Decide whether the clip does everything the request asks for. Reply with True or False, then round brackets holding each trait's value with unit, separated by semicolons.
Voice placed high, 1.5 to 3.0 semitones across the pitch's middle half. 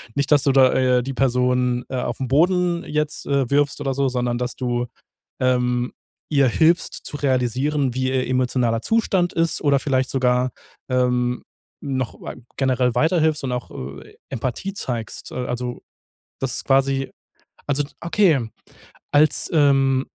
False (130 Hz; 2.6 semitones)